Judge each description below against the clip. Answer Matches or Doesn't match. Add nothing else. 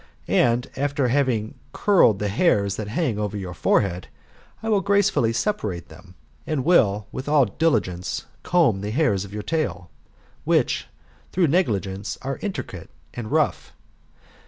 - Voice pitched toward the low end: Matches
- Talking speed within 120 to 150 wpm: Matches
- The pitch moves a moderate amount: Doesn't match